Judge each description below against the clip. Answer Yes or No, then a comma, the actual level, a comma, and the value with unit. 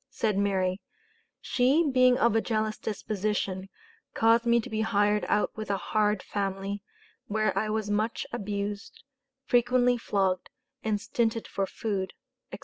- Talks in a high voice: Yes, high, 215 Hz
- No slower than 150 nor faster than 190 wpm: No, average, 140 wpm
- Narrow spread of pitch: Yes, narrow, 2.2 semitones